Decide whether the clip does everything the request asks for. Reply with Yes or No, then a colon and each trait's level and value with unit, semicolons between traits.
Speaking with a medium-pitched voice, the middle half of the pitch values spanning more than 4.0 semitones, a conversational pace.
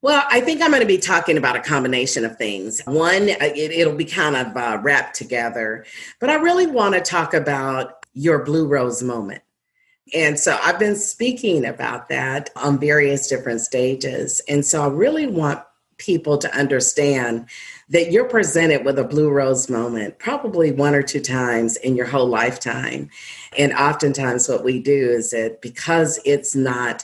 Yes: medium, 145 Hz; average, 5.0 semitones; average, 175 wpm